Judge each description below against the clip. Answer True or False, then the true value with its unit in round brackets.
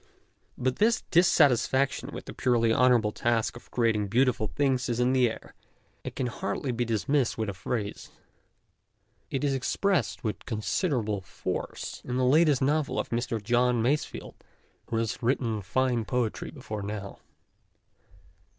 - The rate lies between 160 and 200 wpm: False (150 wpm)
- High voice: False (125 Hz)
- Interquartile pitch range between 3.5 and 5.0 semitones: False (2.9 semitones)